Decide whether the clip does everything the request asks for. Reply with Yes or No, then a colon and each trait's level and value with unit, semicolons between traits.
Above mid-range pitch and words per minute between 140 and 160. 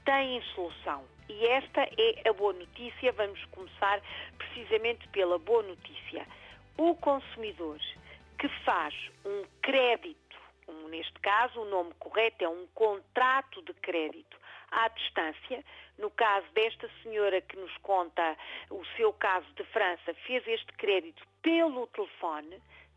No: high, 225 Hz; average, 130 wpm